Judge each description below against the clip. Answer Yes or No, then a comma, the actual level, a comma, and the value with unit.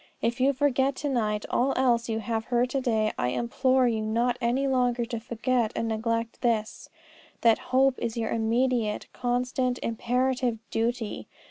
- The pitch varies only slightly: Yes, narrow, 2.1 semitones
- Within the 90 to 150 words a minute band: No, average, 160 wpm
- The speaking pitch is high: Yes, high, 240 Hz